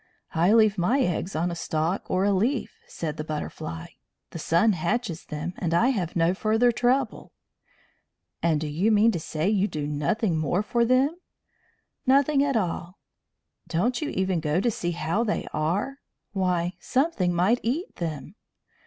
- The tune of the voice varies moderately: No, wide, 5.8 semitones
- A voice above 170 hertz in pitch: Yes, medium, 185 Hz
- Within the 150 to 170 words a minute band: Yes, average, 165 wpm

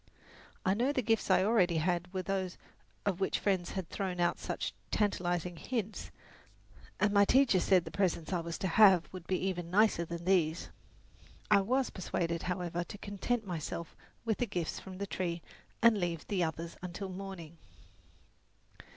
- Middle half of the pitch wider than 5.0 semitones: No, average, 2.8 semitones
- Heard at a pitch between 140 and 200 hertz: Yes, medium, 185 Hz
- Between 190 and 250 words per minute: No, average, 170 wpm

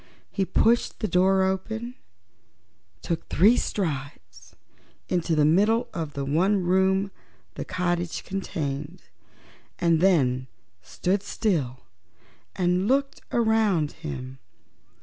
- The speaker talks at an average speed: No, slow, 105 wpm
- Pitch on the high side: No, medium, 180 Hz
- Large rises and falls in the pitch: No, average, 4.7 semitones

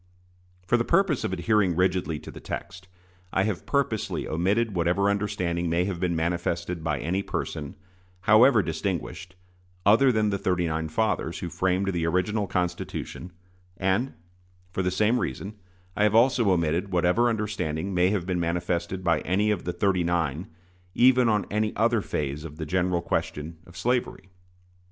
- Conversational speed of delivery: Yes, average, 160 wpm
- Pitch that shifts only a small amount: No, average, 3.6 semitones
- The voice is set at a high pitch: No, very low, 90 Hz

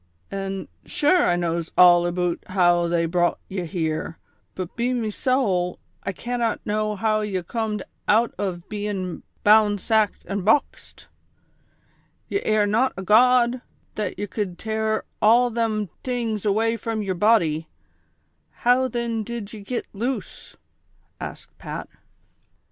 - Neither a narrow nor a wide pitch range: Yes, average, 4.0 semitones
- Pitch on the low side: No, high, 210 Hz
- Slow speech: No, average, 150 wpm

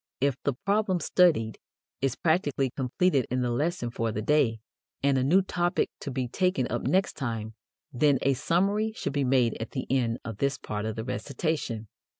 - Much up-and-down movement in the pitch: Yes, wide, 6.1 semitones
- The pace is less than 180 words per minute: No, average, 185 wpm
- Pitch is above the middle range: No, low, 135 Hz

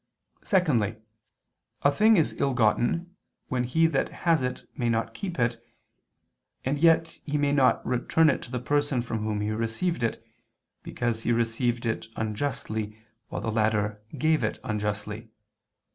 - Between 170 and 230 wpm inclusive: No, average, 155 wpm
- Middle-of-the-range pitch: No, low, 120 Hz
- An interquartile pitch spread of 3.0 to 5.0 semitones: Yes, average, 4.7 semitones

